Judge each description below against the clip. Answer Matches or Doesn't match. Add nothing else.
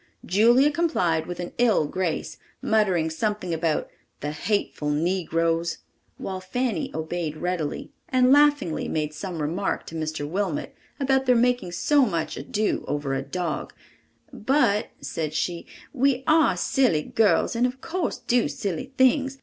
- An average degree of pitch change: Doesn't match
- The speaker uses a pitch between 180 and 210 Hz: Matches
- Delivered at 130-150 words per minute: Matches